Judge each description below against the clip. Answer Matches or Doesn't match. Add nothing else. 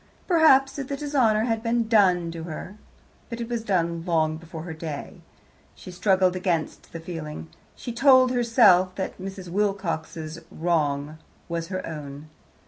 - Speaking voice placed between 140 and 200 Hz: Matches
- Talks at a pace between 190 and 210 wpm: Doesn't match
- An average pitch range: Doesn't match